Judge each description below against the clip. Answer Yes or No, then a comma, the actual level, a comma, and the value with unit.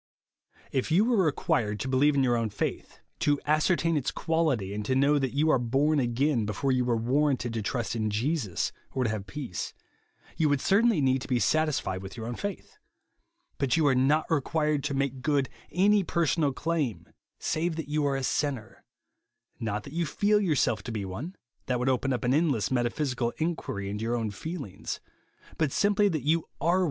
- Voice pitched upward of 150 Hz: No, low, 135 Hz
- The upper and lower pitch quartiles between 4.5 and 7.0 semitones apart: Yes, average, 4.8 semitones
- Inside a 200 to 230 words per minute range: Yes, fast, 205 wpm